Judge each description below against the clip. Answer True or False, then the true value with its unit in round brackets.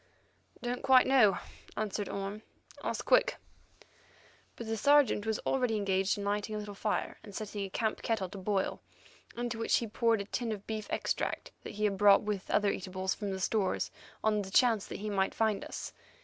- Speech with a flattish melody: True (2.1 semitones)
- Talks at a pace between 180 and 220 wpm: True (190 wpm)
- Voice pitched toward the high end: True (210 Hz)